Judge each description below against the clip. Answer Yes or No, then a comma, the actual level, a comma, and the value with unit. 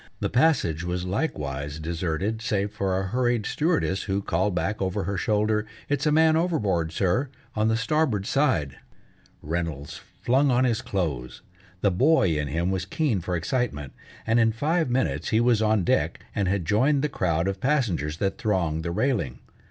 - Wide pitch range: Yes, wide, 6.3 semitones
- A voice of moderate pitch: No, low, 100 Hz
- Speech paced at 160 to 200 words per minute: Yes, average, 175 wpm